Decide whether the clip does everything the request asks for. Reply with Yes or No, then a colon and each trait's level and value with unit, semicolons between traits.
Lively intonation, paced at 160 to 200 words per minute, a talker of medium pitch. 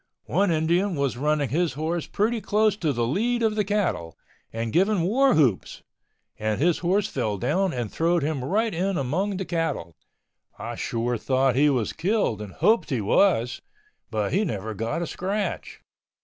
Yes: wide, 8.2 semitones; average, 175 wpm; medium, 165 Hz